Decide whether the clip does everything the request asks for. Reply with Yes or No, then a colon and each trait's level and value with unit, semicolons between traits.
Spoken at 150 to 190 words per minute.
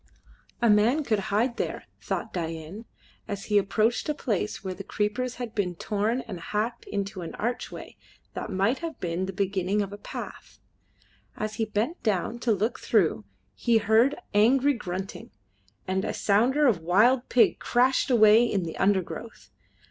Yes: average, 165 wpm